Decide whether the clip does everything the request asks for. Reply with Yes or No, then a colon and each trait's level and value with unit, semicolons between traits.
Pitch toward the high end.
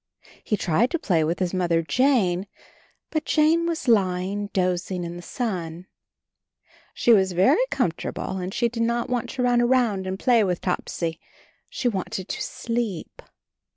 Yes: high, 195 Hz